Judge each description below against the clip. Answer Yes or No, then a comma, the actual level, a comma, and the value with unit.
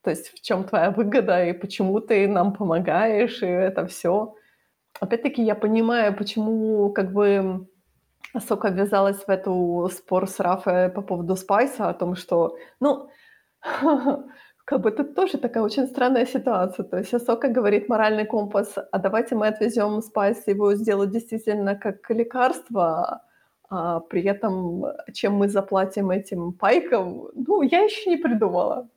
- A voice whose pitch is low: No, high, 210 Hz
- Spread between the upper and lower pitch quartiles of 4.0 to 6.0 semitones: No, average, 3.6 semitones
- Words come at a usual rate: Yes, average, 145 wpm